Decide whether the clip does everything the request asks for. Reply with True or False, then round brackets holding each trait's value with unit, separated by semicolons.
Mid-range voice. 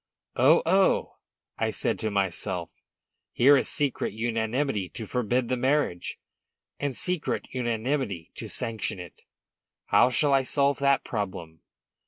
False (120 Hz)